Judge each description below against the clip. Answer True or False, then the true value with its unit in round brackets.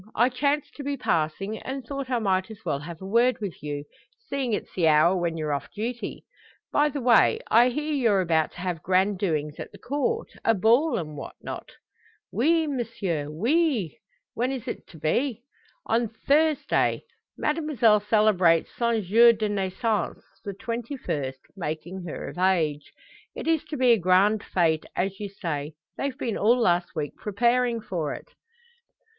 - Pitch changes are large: True (6.3 semitones)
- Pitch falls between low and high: False (210 Hz)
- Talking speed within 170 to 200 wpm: True (175 wpm)